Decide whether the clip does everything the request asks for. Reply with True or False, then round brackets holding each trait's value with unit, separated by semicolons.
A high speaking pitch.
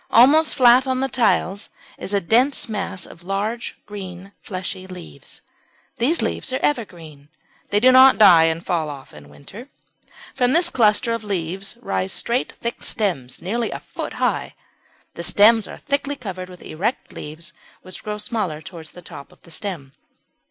True (200 Hz)